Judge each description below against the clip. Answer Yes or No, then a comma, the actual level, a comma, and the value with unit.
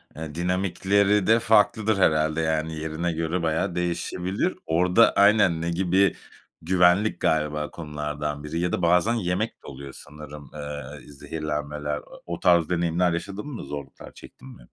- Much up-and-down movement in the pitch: No, average, 3.6 semitones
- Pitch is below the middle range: Yes, very low, 85 Hz